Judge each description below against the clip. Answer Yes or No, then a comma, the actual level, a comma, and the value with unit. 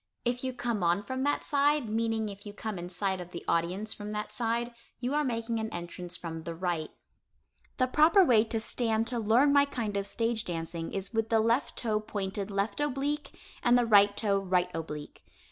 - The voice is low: No, high, 220 Hz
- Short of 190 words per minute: No, fast, 205 wpm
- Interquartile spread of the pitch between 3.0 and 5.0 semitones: Yes, average, 4.2 semitones